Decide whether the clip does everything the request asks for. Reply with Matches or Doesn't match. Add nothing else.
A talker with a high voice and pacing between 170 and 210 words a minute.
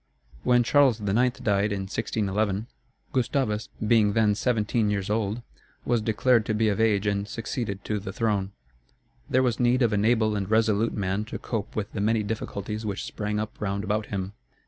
Doesn't match